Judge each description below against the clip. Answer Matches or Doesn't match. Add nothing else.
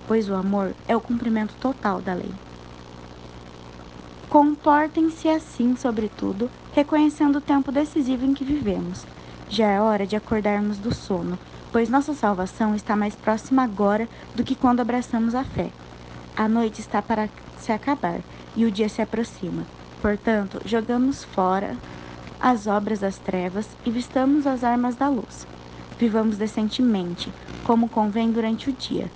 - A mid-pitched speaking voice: Doesn't match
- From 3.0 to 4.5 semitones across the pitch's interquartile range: Matches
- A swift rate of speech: Doesn't match